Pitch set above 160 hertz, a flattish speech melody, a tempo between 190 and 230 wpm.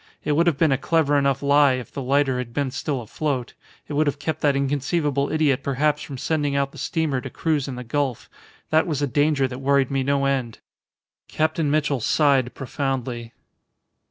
No: medium, 140 Hz; narrow, 2.0 semitones; average, 195 wpm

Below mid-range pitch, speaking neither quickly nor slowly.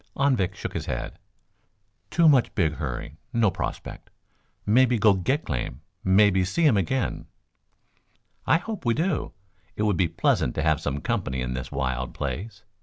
Yes: very low, 95 Hz; average, 160 wpm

